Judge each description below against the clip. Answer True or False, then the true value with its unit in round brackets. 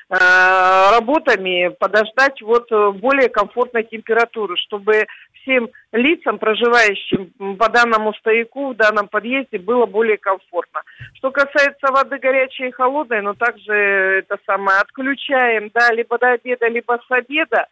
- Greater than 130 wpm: False (125 wpm)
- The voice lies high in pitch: True (230 Hz)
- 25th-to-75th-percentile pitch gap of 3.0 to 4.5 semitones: True (3.5 semitones)